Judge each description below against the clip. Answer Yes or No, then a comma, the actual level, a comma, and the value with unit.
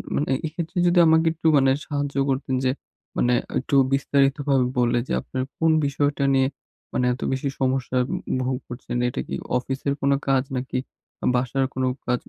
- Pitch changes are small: Yes, narrow, 1.8 semitones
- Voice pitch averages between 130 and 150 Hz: Yes, low, 135 Hz